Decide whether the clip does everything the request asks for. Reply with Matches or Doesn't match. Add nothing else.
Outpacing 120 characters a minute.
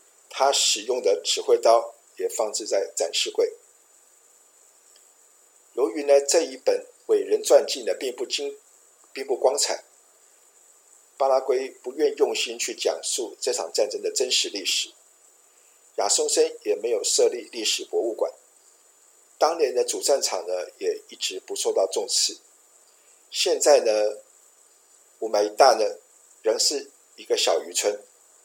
Matches